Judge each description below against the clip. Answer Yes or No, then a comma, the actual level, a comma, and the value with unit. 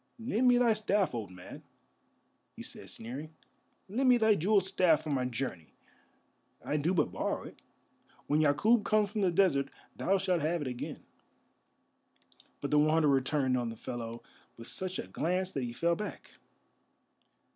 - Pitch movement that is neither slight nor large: No, wide, 7.2 semitones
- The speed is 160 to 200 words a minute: Yes, average, 165 wpm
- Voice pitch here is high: No, medium, 155 Hz